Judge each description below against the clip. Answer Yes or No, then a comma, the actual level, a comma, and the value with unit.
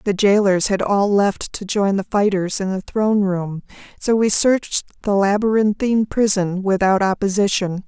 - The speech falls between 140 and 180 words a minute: Yes, average, 160 wpm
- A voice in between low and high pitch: No, high, 200 Hz